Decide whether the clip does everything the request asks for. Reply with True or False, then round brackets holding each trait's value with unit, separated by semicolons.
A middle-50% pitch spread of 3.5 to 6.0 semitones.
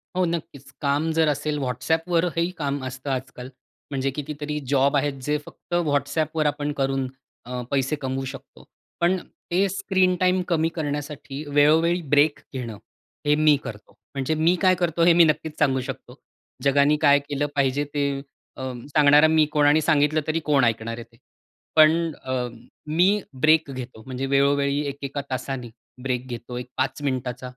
False (2.8 semitones)